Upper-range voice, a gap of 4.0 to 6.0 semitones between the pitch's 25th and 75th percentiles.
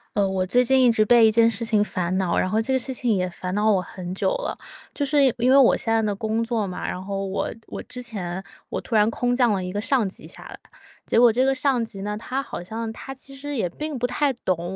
Yes: high, 225 Hz; average, 4.4 semitones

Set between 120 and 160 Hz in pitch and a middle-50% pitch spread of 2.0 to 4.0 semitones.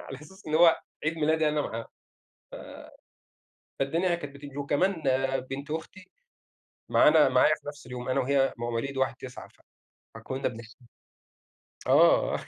Yes: medium, 140 Hz; average, 3.1 semitones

